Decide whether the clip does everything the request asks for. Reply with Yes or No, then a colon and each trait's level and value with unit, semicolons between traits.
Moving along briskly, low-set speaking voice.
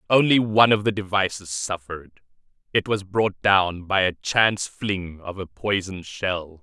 No: average, 165 wpm; very low, 95 Hz